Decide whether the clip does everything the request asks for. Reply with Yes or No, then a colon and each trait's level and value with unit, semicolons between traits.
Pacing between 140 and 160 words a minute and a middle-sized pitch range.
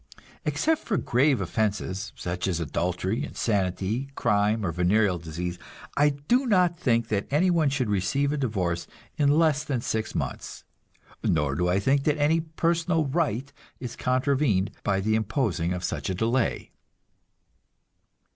No: average, 145 wpm; wide, 7.4 semitones